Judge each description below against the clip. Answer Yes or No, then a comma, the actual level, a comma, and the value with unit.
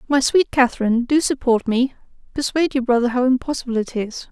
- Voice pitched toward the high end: Yes, very high, 255 Hz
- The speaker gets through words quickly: No, average, 180 wpm